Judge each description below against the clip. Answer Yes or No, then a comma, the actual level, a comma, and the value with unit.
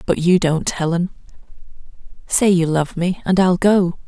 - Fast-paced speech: No, average, 145 wpm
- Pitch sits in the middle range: Yes, medium, 175 Hz